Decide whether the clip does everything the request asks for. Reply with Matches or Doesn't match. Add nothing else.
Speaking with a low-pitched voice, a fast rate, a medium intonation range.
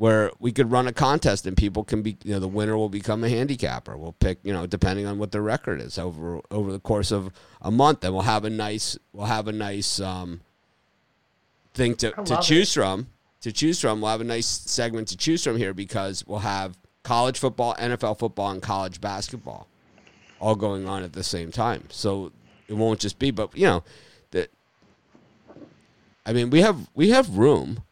Matches